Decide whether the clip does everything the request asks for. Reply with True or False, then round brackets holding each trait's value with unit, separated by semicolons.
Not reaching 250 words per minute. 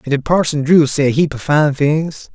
False (255 wpm)